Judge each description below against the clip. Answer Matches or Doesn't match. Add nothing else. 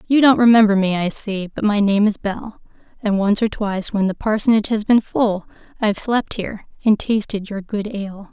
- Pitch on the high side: Matches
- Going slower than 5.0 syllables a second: Doesn't match